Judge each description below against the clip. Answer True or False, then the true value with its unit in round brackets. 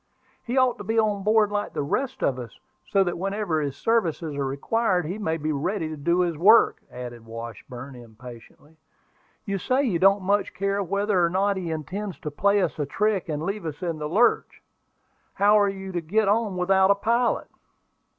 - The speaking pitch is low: False (190 Hz)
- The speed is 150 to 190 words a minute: False (200 wpm)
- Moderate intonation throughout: True (5.0 semitones)